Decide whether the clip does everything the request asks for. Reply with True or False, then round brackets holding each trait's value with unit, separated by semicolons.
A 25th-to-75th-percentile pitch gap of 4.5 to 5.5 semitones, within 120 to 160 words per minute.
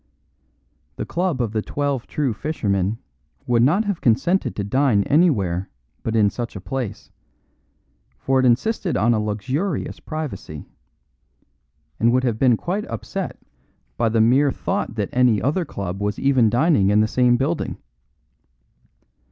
True (5.2 semitones; 145 wpm)